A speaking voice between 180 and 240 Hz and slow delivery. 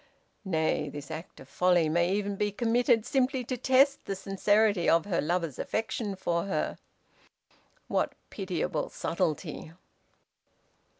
Yes: high, 190 Hz; slow, 125 wpm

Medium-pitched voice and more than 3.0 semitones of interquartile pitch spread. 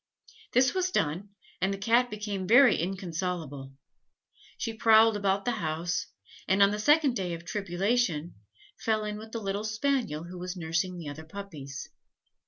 No: high, 195 Hz; average, 4.5 semitones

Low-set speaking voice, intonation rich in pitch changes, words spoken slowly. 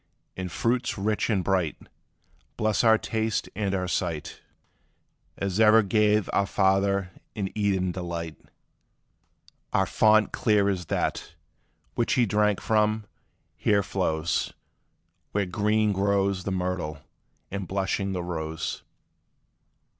No: low, 100 Hz; narrow, 2.6 semitones; slow, 115 wpm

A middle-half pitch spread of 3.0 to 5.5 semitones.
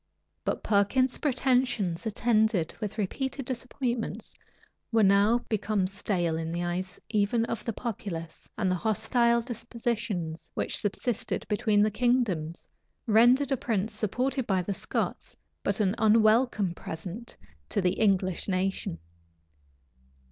Yes: average, 4.0 semitones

